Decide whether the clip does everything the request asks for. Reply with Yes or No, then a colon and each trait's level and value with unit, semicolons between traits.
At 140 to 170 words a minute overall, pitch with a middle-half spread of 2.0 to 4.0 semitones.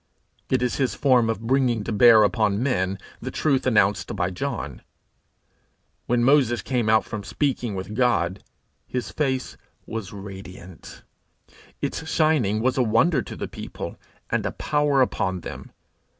No: average, 150 wpm; average, 4.6 semitones